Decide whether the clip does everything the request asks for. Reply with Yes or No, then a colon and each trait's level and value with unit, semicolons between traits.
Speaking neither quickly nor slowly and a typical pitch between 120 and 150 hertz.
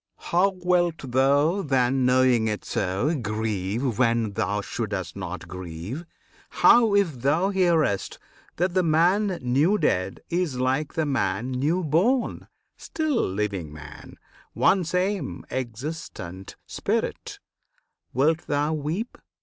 No: slow, 115 wpm; low, 135 Hz